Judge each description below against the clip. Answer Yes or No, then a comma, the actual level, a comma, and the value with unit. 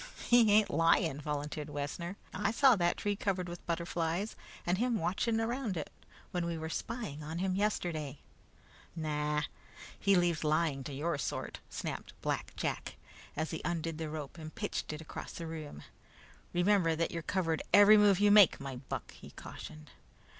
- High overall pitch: No, medium, 170 Hz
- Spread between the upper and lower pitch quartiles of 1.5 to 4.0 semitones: No, average, 4.4 semitones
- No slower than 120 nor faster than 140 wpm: No, average, 170 wpm